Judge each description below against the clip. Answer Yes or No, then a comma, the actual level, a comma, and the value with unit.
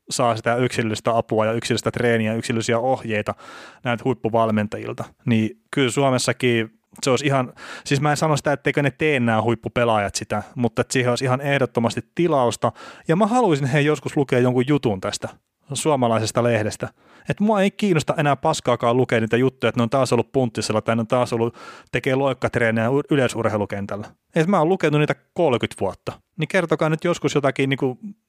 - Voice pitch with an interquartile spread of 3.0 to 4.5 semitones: Yes, average, 4.1 semitones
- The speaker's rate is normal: No, fast, 175 wpm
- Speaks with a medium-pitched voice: No, low, 125 Hz